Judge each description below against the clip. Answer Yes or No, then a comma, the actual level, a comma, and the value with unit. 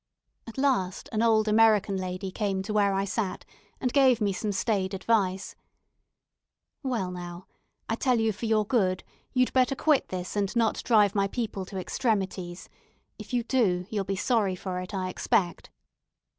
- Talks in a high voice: Yes, high, 205 Hz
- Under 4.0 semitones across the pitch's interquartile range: Yes, average, 3.4 semitones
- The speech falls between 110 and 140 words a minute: No, average, 170 wpm